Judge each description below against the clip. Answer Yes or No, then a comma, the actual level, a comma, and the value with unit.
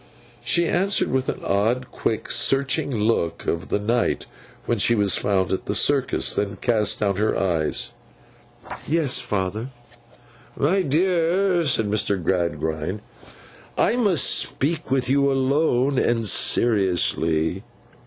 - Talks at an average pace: No, slow, 125 wpm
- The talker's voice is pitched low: Yes, low, 120 Hz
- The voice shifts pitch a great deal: Yes, wide, 6.1 semitones